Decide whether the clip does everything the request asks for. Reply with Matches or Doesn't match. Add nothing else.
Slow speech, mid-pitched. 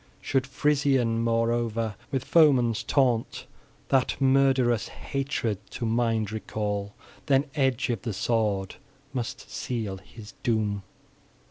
Doesn't match